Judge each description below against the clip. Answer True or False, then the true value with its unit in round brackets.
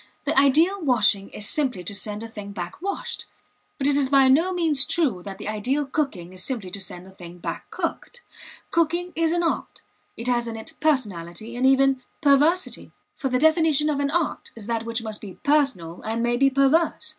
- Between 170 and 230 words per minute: True (205 wpm)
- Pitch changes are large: True (6.4 semitones)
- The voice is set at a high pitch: True (265 Hz)